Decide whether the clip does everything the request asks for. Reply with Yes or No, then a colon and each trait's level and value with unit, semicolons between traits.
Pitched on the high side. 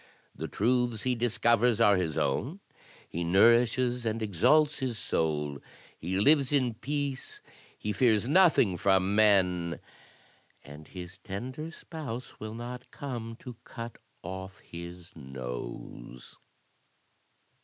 No: low, 110 Hz